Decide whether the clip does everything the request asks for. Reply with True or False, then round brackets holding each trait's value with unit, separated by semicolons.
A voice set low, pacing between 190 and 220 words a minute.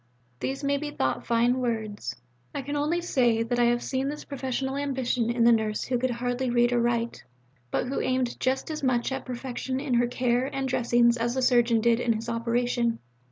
False (245 Hz; 205 wpm)